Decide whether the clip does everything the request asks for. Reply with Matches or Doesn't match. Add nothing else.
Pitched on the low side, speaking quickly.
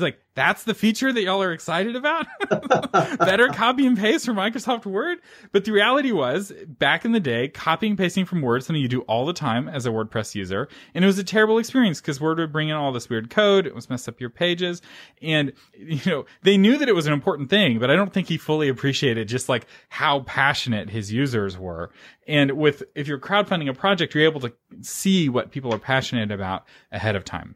Doesn't match